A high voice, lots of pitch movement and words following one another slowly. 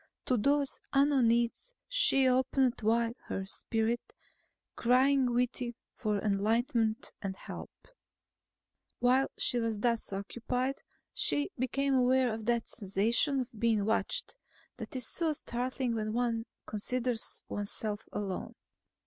No: high, 240 Hz; average, 2.8 semitones; slow, 120 wpm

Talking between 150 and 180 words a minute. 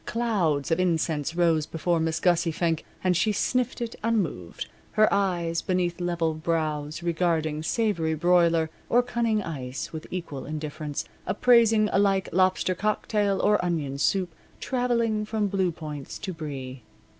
No: average, 140 wpm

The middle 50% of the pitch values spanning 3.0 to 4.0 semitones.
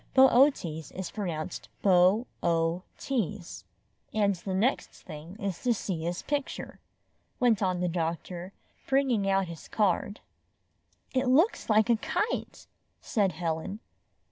No: average, 5.2 semitones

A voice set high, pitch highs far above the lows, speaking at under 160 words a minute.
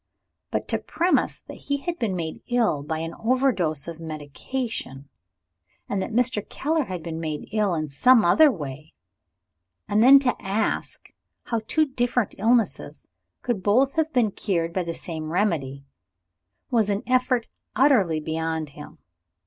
Yes: high, 205 Hz; wide, 7.6 semitones; average, 150 wpm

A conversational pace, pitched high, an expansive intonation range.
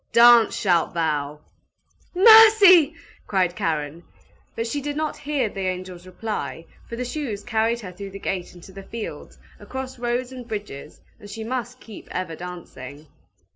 Yes: average, 160 wpm; high, 210 Hz; wide, 5.9 semitones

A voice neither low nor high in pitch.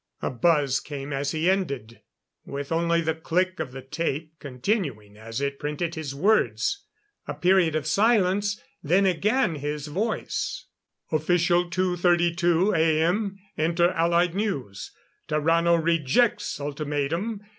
Yes: medium, 165 Hz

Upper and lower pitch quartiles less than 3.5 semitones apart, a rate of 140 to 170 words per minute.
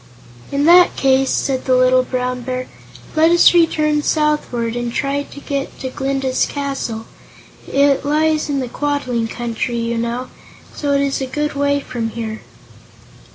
Yes: average, 2.7 semitones; average, 155 wpm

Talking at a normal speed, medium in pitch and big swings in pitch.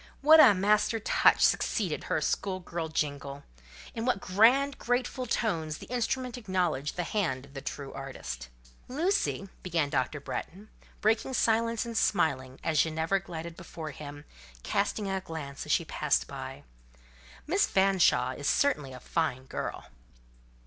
Yes: average, 145 wpm; medium, 175 Hz; wide, 7.6 semitones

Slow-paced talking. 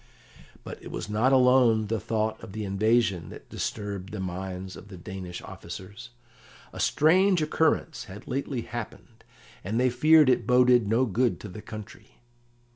No: average, 160 wpm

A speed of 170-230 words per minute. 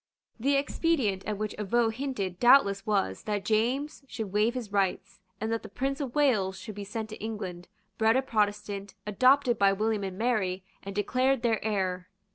Yes: average, 180 wpm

